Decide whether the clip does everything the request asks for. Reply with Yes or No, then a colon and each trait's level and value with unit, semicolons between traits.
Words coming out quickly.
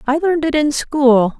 Yes: fast, 215 wpm